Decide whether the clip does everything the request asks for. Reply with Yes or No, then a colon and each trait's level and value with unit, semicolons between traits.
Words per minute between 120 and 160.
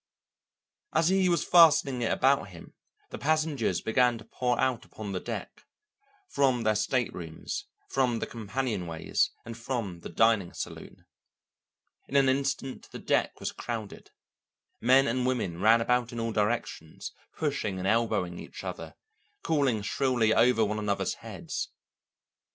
Yes: average, 140 wpm